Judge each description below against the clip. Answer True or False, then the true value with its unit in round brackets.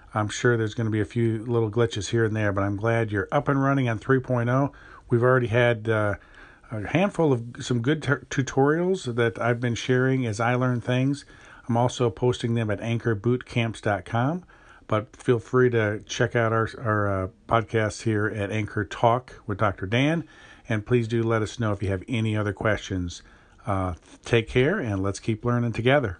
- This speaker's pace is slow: False (190 wpm)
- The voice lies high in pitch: False (115 Hz)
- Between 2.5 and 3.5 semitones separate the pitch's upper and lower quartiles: True (2.9 semitones)